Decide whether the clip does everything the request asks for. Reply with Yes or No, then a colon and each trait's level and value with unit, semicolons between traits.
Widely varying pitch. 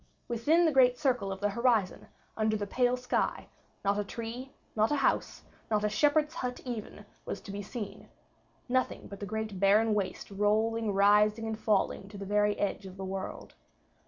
No: average, 3.4 semitones